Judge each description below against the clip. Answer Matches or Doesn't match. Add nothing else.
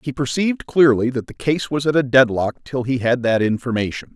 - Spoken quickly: Matches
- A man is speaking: Matches